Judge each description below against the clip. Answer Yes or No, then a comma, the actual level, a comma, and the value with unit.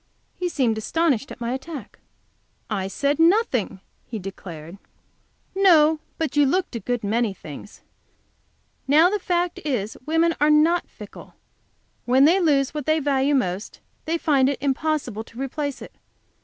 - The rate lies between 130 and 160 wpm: Yes, average, 150 wpm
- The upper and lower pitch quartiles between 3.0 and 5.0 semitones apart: No, wide, 5.5 semitones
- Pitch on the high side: Yes, very high, 280 Hz